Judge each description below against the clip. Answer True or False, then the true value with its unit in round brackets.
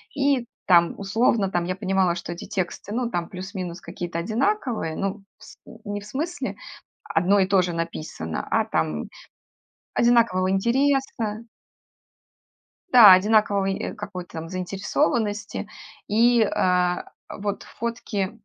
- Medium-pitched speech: False (195 Hz)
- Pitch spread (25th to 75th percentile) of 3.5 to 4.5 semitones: True (4.0 semitones)